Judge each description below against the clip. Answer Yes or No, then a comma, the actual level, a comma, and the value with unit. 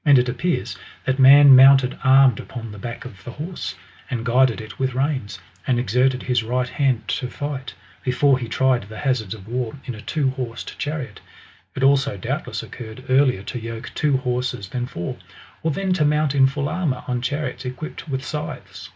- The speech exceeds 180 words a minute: Yes, average, 190 wpm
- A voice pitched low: Yes, low, 130 Hz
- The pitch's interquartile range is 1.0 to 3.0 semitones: Yes, narrow, 2.6 semitones